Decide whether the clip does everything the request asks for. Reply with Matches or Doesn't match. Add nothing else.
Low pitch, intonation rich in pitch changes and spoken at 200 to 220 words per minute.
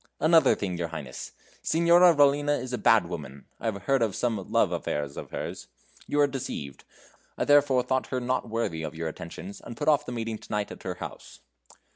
Matches